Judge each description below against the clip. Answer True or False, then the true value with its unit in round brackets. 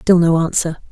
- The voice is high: False (170 Hz)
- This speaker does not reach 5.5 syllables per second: True (5.0 syllables/s)